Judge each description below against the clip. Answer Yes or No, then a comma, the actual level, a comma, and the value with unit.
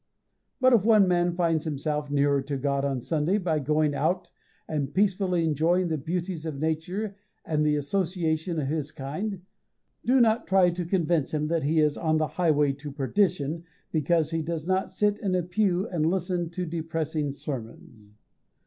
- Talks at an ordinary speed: Yes, average, 170 wpm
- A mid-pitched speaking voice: Yes, medium, 160 Hz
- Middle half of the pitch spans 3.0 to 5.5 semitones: Yes, average, 3.5 semitones